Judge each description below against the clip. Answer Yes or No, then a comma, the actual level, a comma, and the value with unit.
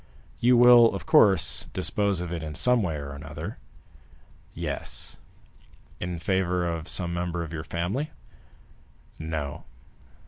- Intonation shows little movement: No, average, 3.9 semitones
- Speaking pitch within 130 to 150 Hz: No, very low, 85 Hz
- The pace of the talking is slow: Yes, slow, 130 wpm